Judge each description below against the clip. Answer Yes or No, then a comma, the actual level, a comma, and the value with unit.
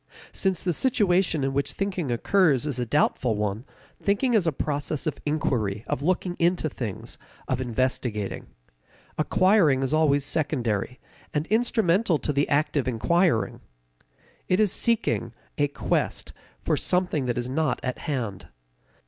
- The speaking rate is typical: Yes, average, 145 wpm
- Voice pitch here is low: No, medium, 145 Hz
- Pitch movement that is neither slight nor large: No, wide, 6.1 semitones